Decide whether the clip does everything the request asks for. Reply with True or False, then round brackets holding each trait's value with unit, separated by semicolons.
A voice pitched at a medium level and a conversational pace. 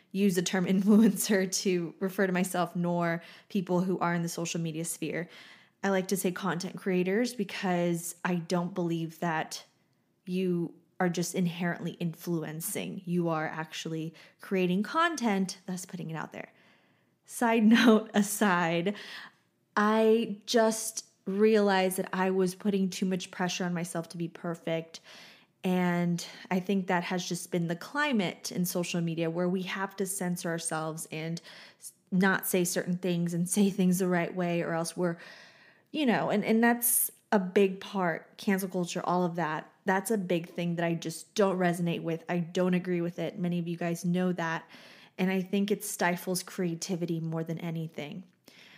True (180 Hz; 165 wpm)